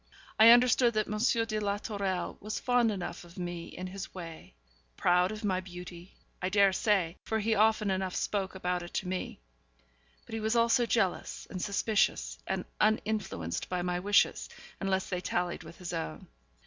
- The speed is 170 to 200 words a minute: Yes, average, 175 wpm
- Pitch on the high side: Yes, high, 195 Hz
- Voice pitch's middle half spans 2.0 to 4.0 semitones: Yes, average, 3.3 semitones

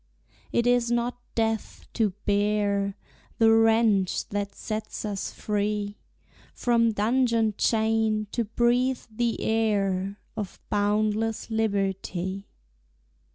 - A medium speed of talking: No, slow, 100 wpm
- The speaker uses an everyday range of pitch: No, narrow, 2.0 semitones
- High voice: Yes, high, 215 Hz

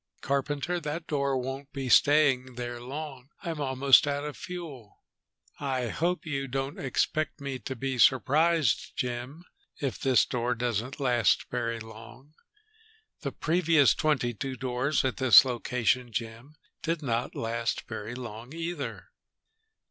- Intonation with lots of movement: No, average, 3.3 semitones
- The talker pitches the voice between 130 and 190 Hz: Yes, low, 135 Hz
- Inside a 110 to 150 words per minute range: Yes, slow, 135 wpm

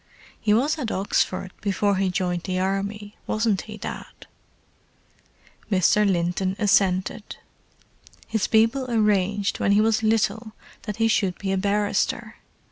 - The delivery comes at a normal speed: No, slow, 130 wpm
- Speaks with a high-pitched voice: Yes, high, 205 Hz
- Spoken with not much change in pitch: Yes, narrow, 2.3 semitones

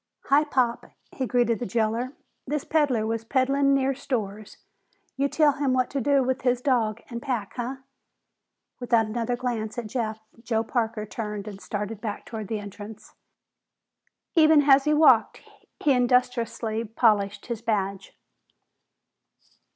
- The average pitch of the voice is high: Yes, high, 235 Hz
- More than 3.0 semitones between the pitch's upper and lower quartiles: Yes, average, 3.4 semitones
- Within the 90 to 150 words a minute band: Yes, average, 145 wpm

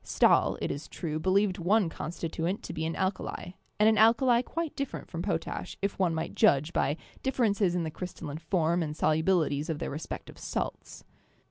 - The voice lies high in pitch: No, medium, 175 Hz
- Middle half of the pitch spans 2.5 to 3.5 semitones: No, average, 4.2 semitones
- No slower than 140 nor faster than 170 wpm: No, average, 190 wpm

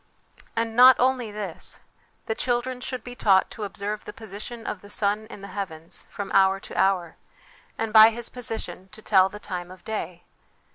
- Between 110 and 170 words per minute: No, average, 185 wpm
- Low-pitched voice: No, high, 210 Hz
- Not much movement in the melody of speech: No, average, 3.0 semitones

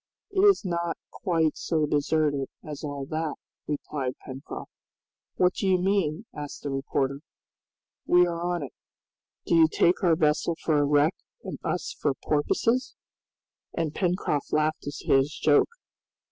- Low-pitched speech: No, medium, 155 Hz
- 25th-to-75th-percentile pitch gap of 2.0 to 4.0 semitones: Yes, average, 3.1 semitones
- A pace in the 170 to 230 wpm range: No, average, 145 wpm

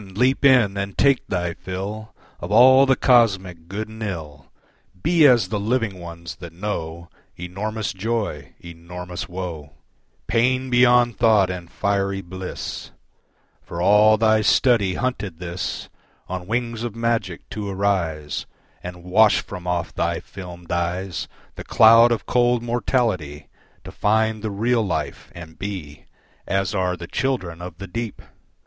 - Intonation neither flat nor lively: Yes, average, 4.5 semitones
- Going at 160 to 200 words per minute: No, average, 140 wpm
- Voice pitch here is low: Yes, low, 100 Hz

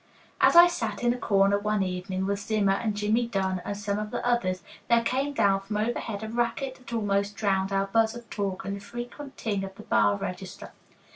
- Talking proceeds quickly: Yes, fast, 215 wpm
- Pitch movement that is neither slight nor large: Yes, average, 3.0 semitones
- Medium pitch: No, high, 205 Hz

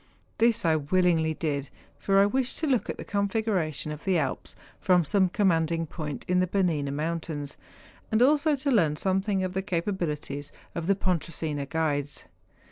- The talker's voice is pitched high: No, medium, 175 Hz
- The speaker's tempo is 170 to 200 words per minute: Yes, average, 175 wpm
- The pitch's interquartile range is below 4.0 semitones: No, average, 4.4 semitones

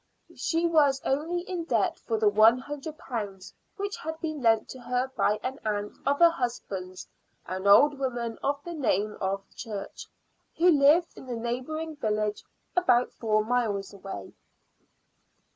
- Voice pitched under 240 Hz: No, high, 245 Hz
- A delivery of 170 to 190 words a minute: No, average, 155 wpm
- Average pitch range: No, wide, 6.4 semitones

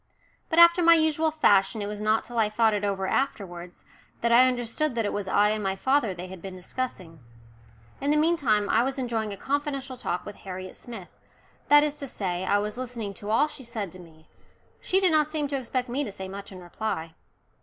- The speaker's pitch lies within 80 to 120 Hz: No, high, 225 Hz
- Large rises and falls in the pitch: Yes, wide, 6.1 semitones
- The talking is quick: Yes, fast, 220 wpm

